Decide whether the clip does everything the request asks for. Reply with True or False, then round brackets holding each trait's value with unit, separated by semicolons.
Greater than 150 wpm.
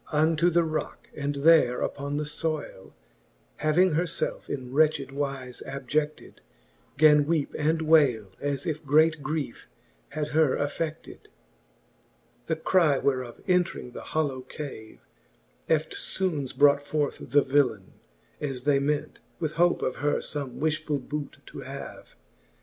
False (135 wpm)